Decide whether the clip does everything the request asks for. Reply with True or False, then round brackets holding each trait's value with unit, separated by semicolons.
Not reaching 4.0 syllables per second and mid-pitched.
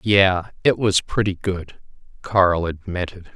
False (3.8 syllables/s; 95 Hz)